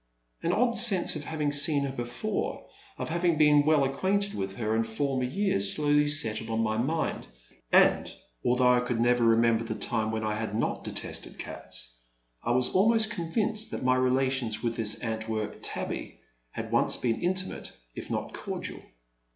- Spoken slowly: No, average, 175 wpm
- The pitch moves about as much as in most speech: No, wide, 5.9 semitones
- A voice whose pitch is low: Yes, low, 130 Hz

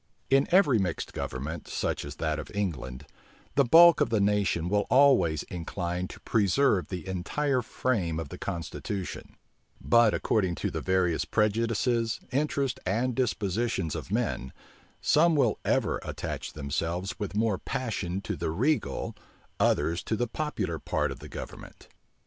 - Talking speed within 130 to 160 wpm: Yes, average, 150 wpm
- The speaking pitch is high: No, low, 100 Hz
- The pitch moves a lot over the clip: Yes, wide, 6.3 semitones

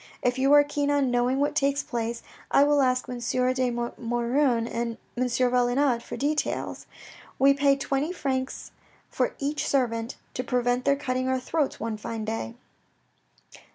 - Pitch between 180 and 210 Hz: No, very high, 255 Hz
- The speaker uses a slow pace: No, average, 155 wpm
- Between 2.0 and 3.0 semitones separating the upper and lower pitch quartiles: Yes, narrow, 2.6 semitones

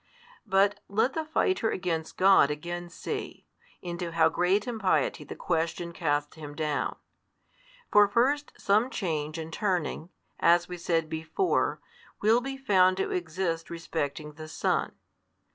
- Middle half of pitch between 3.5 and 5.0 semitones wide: Yes, average, 4.2 semitones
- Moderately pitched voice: Yes, medium, 175 Hz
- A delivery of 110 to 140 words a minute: Yes, slow, 135 wpm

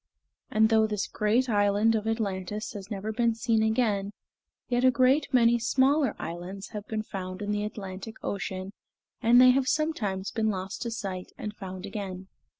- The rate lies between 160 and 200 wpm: Yes, average, 170 wpm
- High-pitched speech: Yes, high, 215 Hz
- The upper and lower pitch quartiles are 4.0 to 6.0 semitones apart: No, average, 3.0 semitones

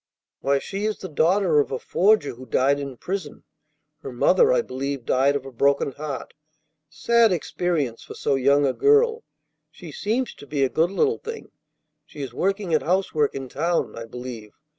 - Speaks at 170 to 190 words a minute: Yes, average, 185 wpm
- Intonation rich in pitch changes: Yes, wide, 6.3 semitones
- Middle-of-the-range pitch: Yes, medium, 150 Hz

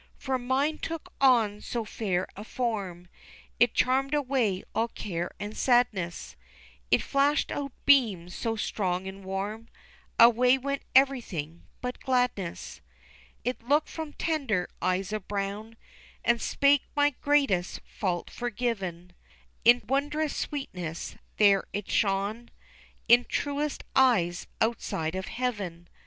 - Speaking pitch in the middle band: No, high, 230 Hz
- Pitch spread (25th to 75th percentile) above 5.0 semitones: Yes, wide, 5.6 semitones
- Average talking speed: No, slow, 120 wpm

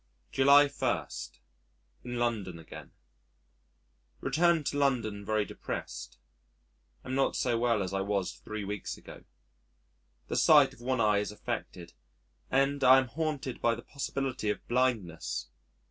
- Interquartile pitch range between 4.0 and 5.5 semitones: Yes, average, 4.7 semitones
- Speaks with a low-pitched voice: Yes, low, 120 Hz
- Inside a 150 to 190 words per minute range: No, slow, 135 wpm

